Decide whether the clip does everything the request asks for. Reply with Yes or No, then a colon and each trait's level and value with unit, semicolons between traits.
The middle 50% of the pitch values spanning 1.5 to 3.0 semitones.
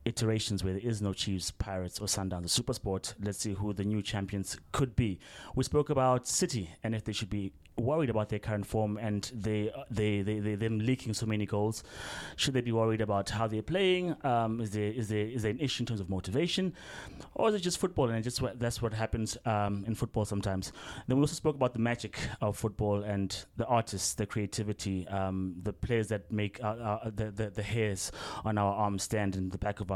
Yes: narrow, 2.6 semitones